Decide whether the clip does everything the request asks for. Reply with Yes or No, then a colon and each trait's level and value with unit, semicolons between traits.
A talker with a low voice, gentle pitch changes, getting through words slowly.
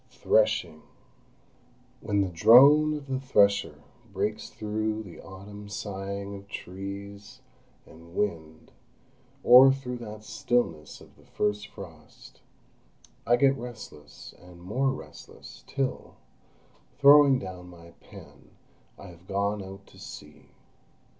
No: low, 100 Hz; average, 4.4 semitones; slow, 115 wpm